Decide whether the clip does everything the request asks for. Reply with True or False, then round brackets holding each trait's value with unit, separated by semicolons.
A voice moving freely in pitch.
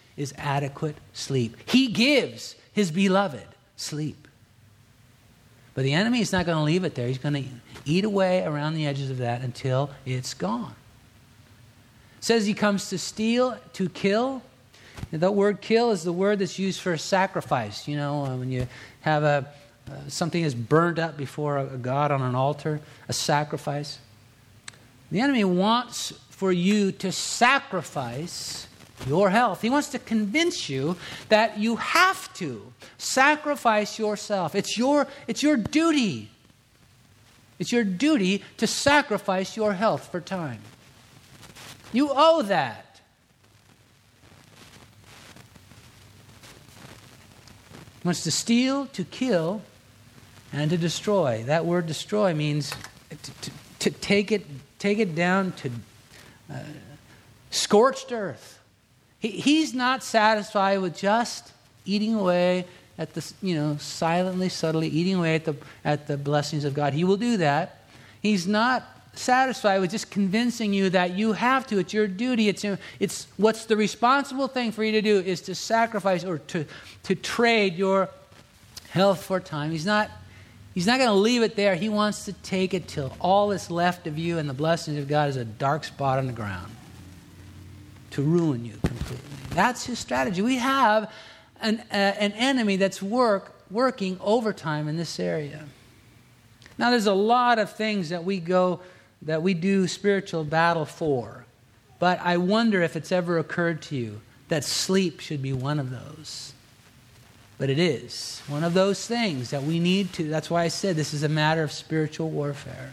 True (7.4 semitones)